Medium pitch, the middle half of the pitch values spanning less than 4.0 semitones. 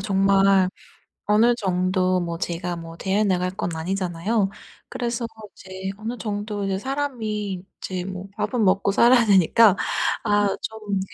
No: high, 195 Hz; narrow, 2.6 semitones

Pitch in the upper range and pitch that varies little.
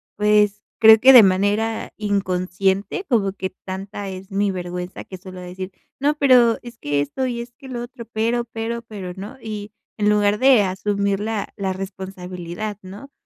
No: high, 205 Hz; average, 3.2 semitones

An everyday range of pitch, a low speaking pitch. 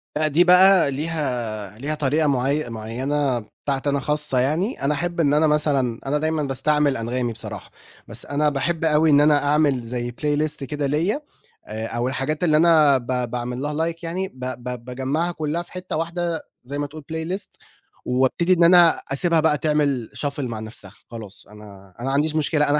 No: average, 3.9 semitones; medium, 145 Hz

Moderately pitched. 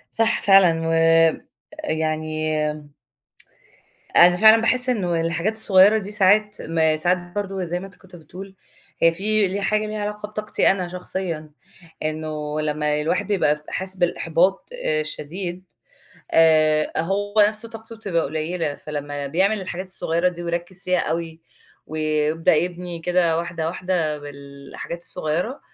Yes: medium, 175 Hz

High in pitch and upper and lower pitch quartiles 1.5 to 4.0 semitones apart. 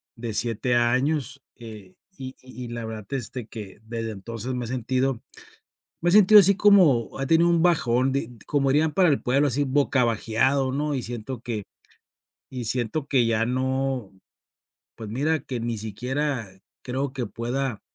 No: low, 125 Hz; average, 3.3 semitones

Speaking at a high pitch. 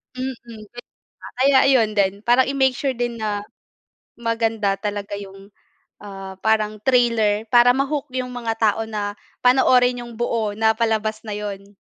Yes: high, 225 Hz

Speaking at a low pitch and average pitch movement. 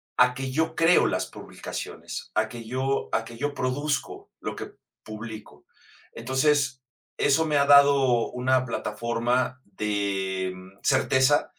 Yes: low, 130 Hz; average, 3.9 semitones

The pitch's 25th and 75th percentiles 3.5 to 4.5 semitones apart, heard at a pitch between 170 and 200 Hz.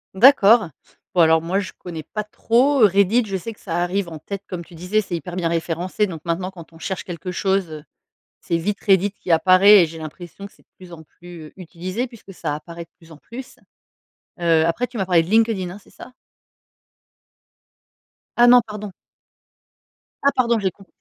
Yes: average, 3.8 semitones; medium, 185 Hz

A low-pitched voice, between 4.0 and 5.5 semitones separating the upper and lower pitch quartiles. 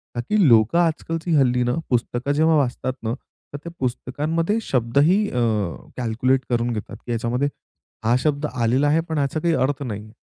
Yes: low, 130 Hz; average, 4.5 semitones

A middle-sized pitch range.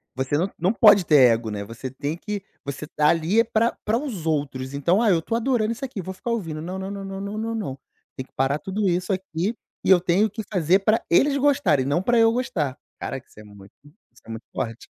No: wide, 7.4 semitones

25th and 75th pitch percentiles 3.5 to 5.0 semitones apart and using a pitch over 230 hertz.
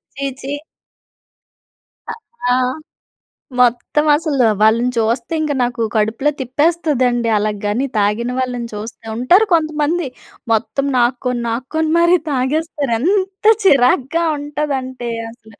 Yes: average, 4.2 semitones; very high, 255 Hz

